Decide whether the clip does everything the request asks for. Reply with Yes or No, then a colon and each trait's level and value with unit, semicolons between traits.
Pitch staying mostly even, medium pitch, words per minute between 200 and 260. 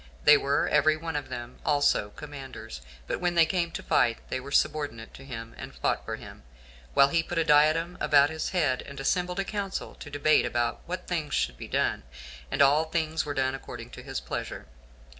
No: average, 3.7 semitones; medium, 145 Hz; fast, 205 wpm